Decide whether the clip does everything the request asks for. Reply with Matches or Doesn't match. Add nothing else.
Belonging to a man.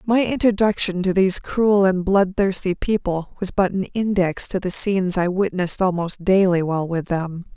Doesn't match